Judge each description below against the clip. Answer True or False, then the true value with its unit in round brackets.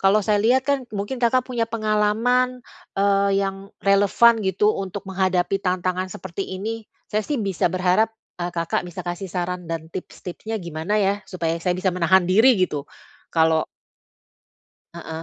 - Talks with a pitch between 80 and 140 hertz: False (190 Hz)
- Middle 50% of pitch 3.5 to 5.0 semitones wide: False (3.1 semitones)